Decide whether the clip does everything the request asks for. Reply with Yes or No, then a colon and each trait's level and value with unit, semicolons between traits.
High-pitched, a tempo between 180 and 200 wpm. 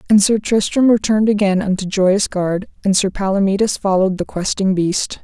No: high, 200 Hz; average, 170 wpm